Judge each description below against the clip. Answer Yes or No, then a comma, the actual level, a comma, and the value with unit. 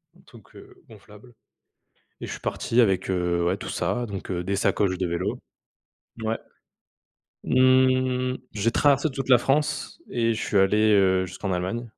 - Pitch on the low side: Yes, low, 110 Hz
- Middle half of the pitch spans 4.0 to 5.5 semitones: Yes, average, 5.2 semitones